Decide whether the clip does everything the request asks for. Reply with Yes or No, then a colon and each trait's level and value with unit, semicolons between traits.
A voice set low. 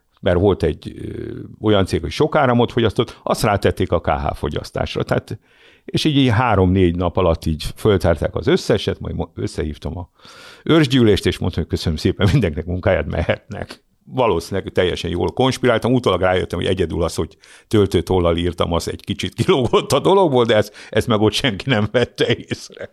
Yes: low, 105 Hz